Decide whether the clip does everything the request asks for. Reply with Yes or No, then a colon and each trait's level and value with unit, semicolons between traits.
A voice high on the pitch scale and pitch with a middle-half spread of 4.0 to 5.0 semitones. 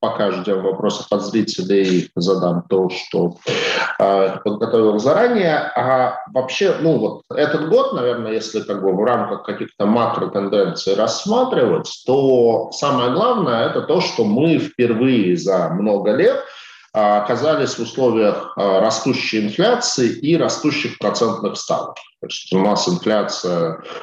No: low, 110 Hz; average, 4.6 semitones